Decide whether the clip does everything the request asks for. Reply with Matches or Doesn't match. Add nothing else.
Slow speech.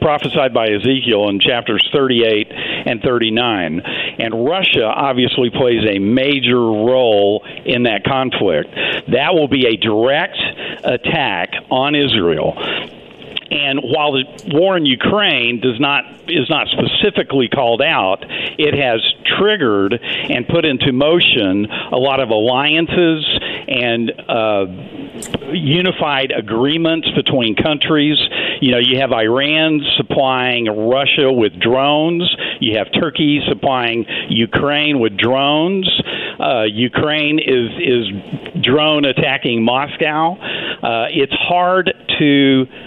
Matches